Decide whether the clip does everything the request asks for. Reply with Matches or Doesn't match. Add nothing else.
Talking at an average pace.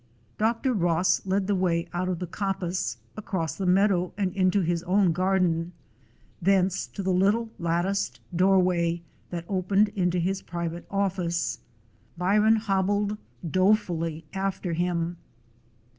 Doesn't match